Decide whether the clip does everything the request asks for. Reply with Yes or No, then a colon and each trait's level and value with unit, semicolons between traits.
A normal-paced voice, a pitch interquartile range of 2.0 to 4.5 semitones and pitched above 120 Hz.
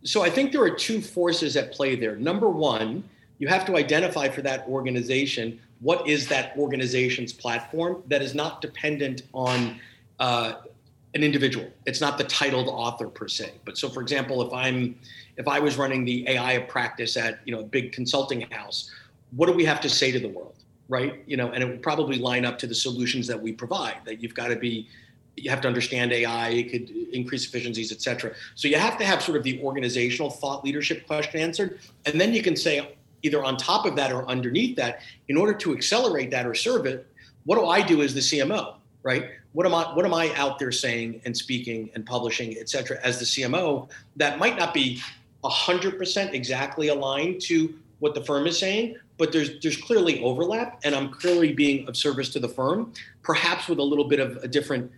No: fast, 210 wpm; average, 3.7 semitones; low, 135 Hz